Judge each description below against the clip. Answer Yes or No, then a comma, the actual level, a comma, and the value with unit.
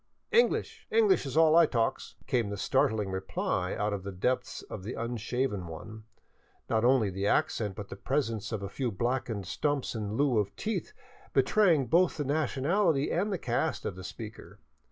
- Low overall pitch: Yes, low, 120 Hz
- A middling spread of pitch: No, wide, 6.2 semitones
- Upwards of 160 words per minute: Yes, average, 180 wpm